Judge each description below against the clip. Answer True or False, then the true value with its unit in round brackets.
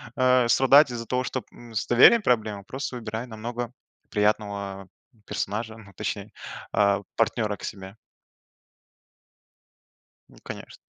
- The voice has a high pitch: False (115 Hz)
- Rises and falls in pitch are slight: False (3.1 semitones)